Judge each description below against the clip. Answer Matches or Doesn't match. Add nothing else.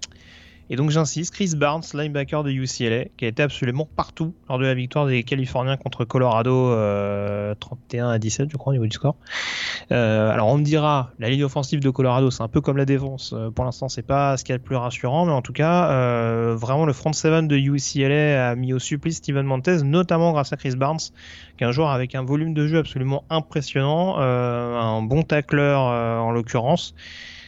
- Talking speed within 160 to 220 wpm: Matches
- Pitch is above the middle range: Doesn't match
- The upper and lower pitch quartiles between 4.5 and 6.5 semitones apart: Doesn't match